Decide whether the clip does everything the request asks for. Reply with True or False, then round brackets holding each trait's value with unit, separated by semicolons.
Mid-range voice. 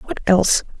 False (230 Hz)